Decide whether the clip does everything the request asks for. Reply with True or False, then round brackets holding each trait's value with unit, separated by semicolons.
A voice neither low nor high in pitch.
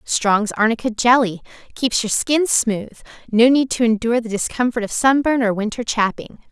False (230 Hz)